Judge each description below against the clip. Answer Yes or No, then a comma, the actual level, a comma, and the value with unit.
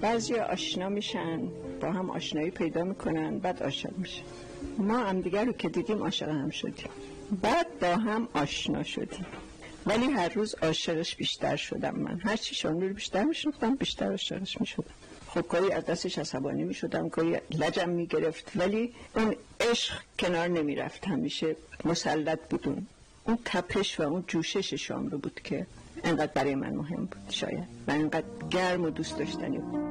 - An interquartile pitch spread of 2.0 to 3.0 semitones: No, average, 4.9 semitones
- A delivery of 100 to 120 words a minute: No, fast, 155 wpm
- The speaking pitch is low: No, medium, 185 Hz